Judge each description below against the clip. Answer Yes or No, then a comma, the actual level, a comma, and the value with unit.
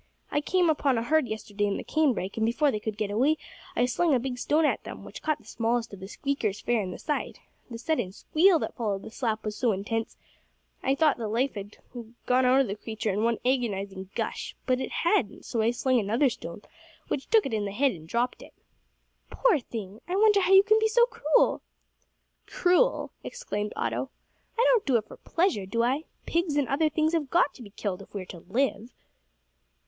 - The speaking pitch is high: Yes, high, 245 Hz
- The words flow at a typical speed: No, fast, 225 wpm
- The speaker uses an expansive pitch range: Yes, wide, 6.5 semitones